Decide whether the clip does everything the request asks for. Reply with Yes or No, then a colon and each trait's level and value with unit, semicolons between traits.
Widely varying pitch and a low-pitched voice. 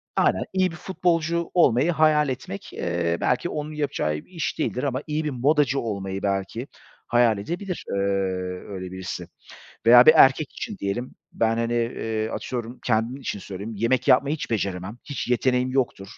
Yes: wide, 5.8 semitones; low, 125 Hz